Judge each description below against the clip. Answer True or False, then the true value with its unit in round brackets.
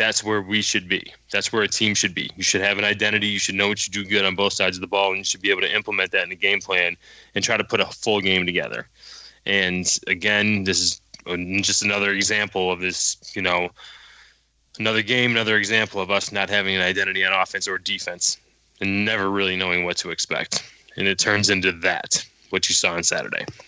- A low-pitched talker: True (100 Hz)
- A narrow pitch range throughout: True (1.9 semitones)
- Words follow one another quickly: True (230 wpm)